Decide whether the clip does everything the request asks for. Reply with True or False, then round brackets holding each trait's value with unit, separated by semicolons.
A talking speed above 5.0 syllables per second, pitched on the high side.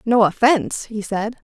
False (4.7 syllables/s; 220 Hz)